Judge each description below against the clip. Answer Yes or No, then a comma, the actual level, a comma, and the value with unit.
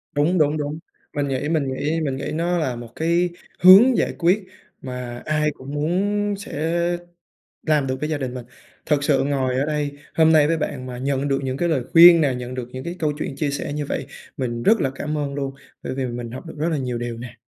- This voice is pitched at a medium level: Yes, medium, 145 Hz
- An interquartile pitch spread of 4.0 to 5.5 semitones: No, average, 3.5 semitones